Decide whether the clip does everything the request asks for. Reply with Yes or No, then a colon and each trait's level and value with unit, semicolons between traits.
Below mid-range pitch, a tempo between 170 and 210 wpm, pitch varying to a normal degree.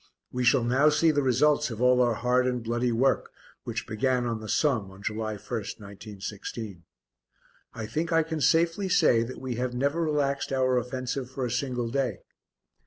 Yes: low, 125 Hz; average, 180 wpm; average, 3.3 semitones